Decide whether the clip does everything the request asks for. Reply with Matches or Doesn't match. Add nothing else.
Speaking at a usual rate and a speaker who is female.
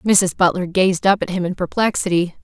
Matches